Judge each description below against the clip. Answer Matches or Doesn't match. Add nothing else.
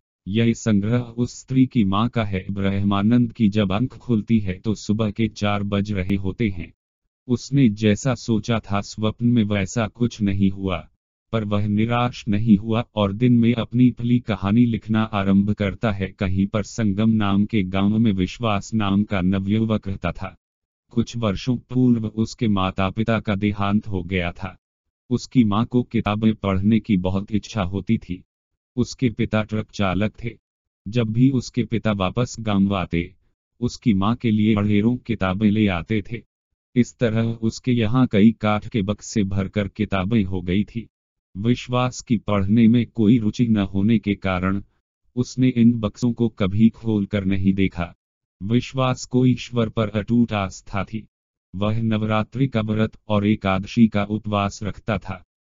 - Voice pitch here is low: Matches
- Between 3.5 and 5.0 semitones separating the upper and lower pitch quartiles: Doesn't match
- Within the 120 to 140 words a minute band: Doesn't match